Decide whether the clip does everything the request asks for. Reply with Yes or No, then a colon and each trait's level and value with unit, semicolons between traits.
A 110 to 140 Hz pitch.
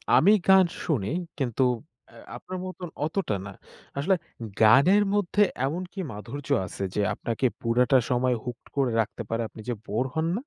Yes: low, 135 Hz